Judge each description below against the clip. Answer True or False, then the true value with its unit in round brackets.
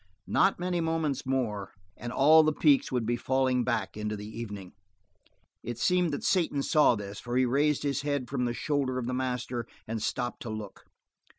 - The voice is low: True (125 Hz)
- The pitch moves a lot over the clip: False (3.7 semitones)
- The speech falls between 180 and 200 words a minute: True (190 wpm)